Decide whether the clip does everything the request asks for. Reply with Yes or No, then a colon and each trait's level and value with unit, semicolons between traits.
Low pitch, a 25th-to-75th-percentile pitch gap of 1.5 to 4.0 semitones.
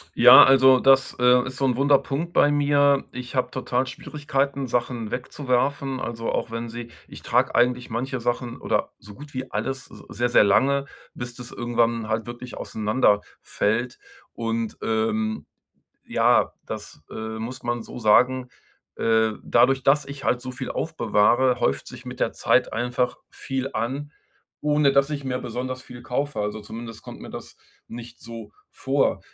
Yes: low, 125 Hz; narrow, 2.6 semitones